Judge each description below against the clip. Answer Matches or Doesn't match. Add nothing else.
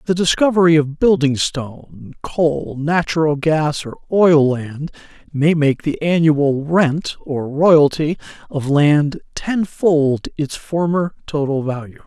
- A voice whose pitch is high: Doesn't match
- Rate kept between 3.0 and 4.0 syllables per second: Matches